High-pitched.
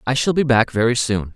No: low, 120 Hz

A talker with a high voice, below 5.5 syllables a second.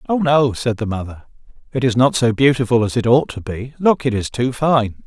No: low, 125 Hz; 5.3 syllables/s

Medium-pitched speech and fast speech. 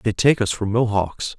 No: low, 110 Hz; fast, 215 wpm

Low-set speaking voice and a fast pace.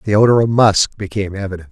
Yes: low, 105 Hz; fast, 210 wpm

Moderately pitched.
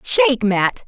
No: very high, 255 Hz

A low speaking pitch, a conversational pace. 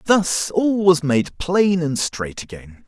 No: medium, 165 Hz; average, 165 wpm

